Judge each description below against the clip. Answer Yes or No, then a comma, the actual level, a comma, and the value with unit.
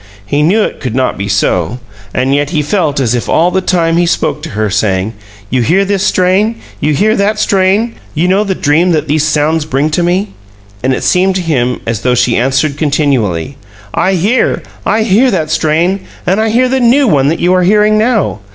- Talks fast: Yes, fast, 215 wpm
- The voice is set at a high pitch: No, medium, 165 Hz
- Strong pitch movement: Yes, wide, 6.3 semitones